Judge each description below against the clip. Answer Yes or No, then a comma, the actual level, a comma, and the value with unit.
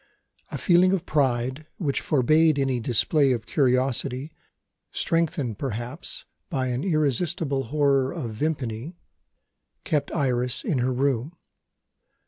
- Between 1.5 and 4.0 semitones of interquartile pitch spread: Yes, average, 3.7 semitones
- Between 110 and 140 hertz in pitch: Yes, low, 135 Hz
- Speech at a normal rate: No, slow, 110 wpm